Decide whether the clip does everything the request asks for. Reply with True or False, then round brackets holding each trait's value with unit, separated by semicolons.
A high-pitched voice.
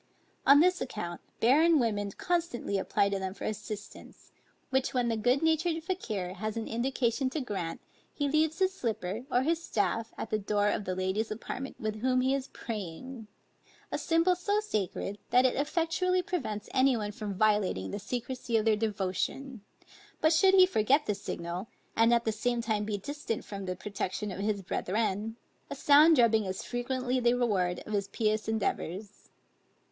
True (225 Hz)